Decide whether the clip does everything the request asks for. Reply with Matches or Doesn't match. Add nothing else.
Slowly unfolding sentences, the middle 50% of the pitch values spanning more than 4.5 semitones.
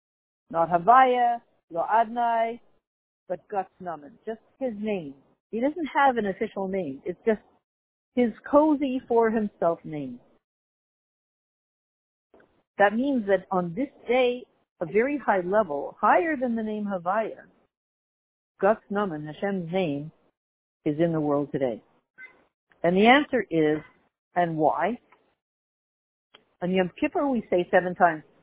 Matches